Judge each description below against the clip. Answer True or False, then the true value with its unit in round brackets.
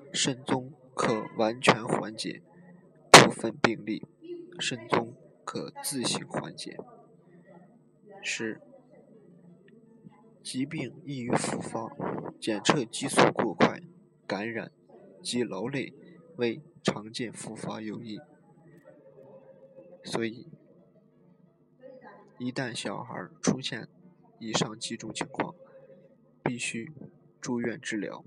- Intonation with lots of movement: True (7.2 semitones)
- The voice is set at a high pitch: False (165 Hz)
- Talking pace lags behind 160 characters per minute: True (135 characters per minute)